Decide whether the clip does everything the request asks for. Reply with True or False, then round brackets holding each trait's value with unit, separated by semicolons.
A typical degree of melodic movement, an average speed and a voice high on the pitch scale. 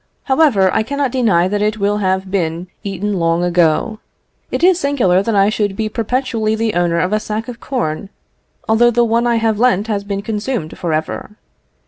True (3.7 semitones; 190 wpm; 210 Hz)